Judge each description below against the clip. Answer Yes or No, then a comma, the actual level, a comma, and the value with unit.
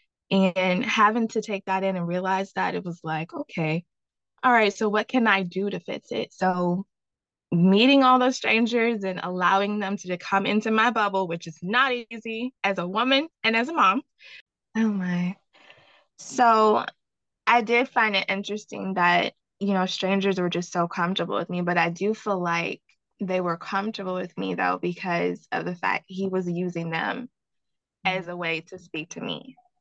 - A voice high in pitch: Yes, high, 195 Hz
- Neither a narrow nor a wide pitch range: Yes, average, 4.0 semitones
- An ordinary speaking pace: Yes, average, 185 wpm